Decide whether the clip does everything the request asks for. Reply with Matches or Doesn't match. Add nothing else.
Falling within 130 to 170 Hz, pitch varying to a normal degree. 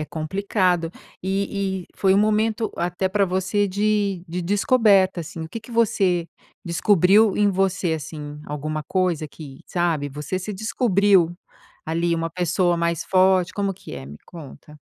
Doesn't match